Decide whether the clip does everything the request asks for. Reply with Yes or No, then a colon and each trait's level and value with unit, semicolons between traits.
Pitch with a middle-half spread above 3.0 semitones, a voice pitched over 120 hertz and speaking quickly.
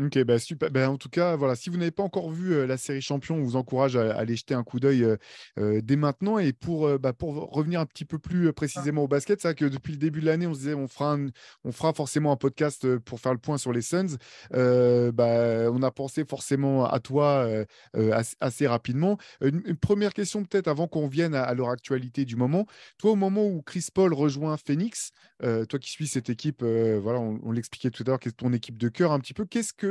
Yes: average, 4.5 semitones; medium, 140 Hz; fast, 255 wpm